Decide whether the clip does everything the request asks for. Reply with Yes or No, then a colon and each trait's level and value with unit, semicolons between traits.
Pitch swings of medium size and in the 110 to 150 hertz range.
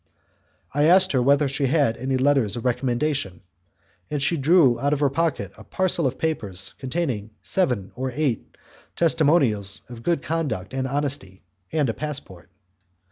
Yes: average, 4.2 semitones; low, 135 Hz